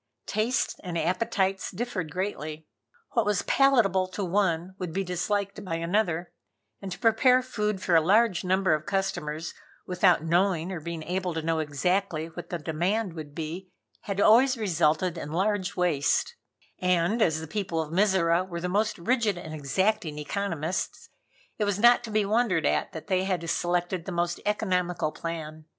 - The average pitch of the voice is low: No, medium, 180 Hz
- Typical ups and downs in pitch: Yes, average, 3.6 semitones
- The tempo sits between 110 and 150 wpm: No, average, 170 wpm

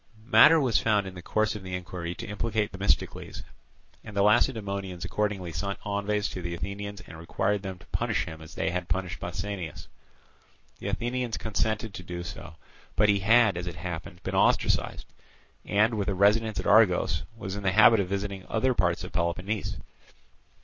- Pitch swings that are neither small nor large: Yes, average, 3.0 semitones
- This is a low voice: Yes, low, 100 Hz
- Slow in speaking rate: No, average, 180 wpm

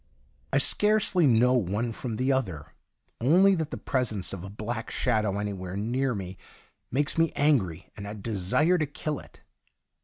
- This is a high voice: No, low, 115 Hz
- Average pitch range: No, wide, 6.2 semitones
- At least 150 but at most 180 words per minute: Yes, average, 160 wpm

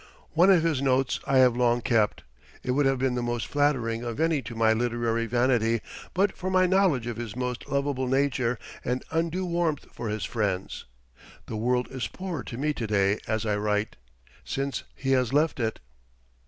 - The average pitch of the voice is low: Yes, low, 125 Hz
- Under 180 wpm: No, average, 190 wpm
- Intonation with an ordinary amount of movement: Yes, average, 3.9 semitones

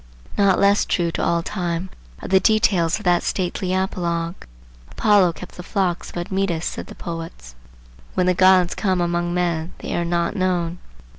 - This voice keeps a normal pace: Yes, average, 170 wpm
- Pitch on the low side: No, medium, 180 Hz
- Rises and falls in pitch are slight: Yes, narrow, 1.7 semitones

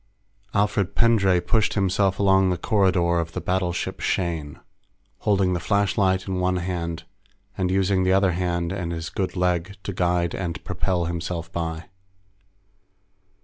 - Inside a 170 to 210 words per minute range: No, average, 145 wpm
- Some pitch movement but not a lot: No, narrow, 2.0 semitones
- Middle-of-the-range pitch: No, very low, 90 Hz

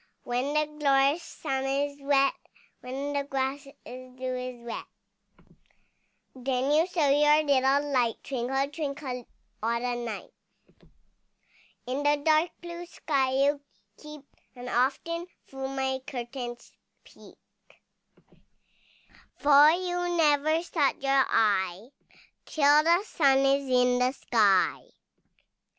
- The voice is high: Yes, very high, 275 Hz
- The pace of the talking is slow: Yes, slow, 115 wpm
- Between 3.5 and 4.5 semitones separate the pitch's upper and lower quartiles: No, average, 2.8 semitones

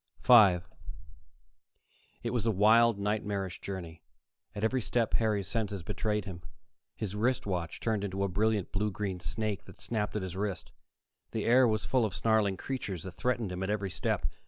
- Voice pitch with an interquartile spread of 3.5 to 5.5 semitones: No, narrow, 2.6 semitones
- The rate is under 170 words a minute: No, average, 175 wpm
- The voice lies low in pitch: Yes, low, 105 Hz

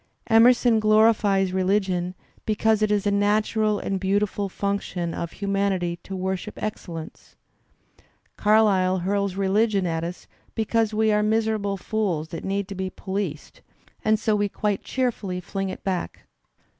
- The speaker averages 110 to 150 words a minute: Yes, average, 140 wpm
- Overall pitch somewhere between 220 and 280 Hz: No, high, 200 Hz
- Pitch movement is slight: Yes, narrow, 2.3 semitones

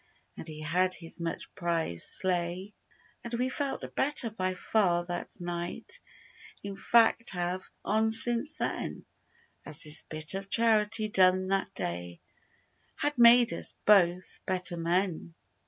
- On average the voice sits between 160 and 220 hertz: Yes, medium, 185 Hz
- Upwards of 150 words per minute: No, slow, 135 wpm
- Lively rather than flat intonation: No, average, 4.4 semitones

